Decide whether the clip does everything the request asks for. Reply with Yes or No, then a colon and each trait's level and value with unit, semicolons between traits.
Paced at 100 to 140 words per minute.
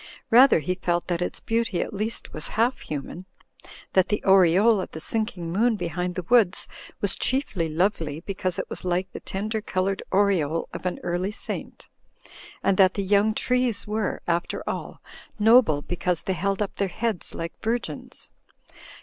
No: average, 165 wpm